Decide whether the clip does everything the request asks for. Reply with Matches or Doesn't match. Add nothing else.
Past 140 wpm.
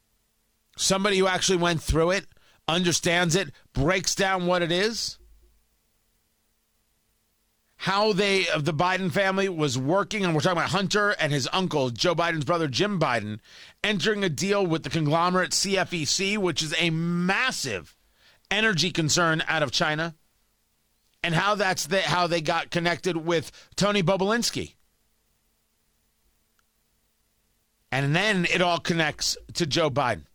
Doesn't match